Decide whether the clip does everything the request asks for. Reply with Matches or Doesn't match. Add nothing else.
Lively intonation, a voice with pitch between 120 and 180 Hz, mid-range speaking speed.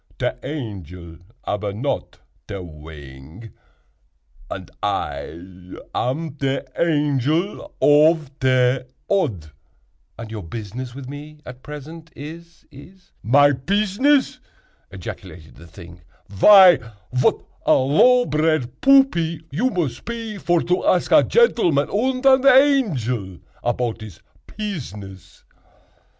Doesn't match